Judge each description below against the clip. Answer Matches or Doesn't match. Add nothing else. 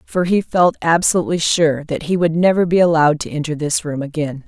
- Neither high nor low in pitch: Matches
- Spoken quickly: Matches